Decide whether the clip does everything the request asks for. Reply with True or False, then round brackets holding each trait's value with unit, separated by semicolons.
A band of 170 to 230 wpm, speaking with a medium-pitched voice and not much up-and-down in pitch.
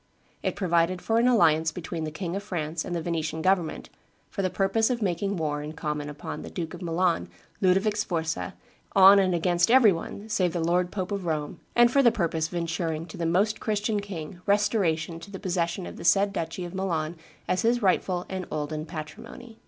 False (205 wpm; 175 Hz; 3.6 semitones)